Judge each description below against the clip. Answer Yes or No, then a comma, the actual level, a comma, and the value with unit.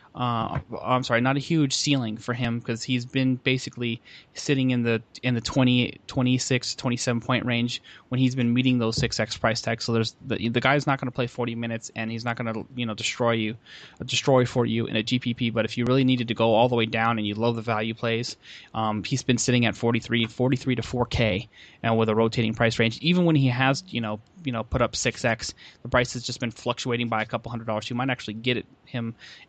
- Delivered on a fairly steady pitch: Yes, narrow, 1.9 semitones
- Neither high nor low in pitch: No, low, 120 Hz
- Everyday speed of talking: No, fast, 240 wpm